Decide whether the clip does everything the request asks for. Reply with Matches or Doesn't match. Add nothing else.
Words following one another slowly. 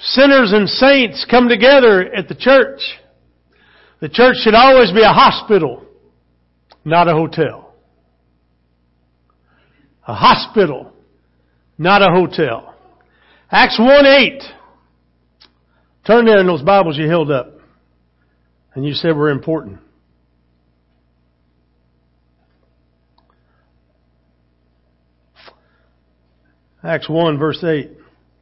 Matches